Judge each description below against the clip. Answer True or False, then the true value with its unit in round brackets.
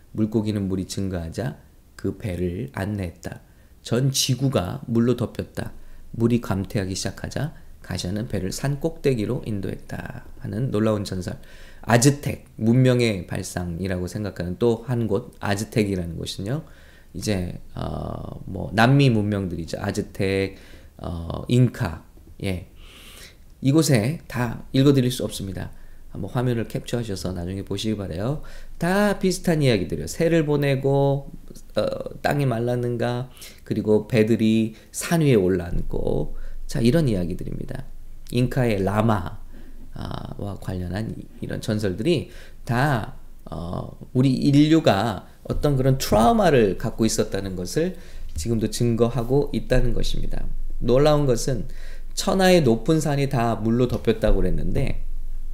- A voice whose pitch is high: False (110 Hz)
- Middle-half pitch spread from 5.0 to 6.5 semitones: True (5.5 semitones)